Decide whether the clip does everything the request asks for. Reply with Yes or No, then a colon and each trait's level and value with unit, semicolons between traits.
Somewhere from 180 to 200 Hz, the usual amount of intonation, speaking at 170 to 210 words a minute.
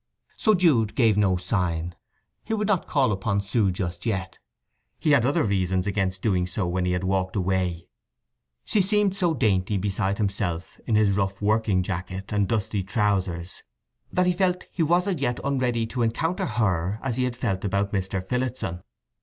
No: low, 100 Hz; average, 5.0 semitones; average, 180 wpm